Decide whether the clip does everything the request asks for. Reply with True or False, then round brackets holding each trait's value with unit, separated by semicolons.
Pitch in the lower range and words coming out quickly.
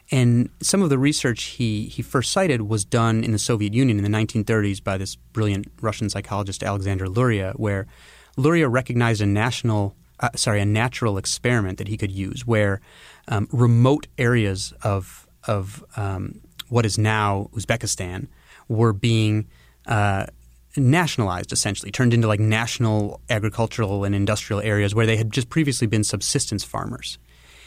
False (110 Hz; 155 wpm)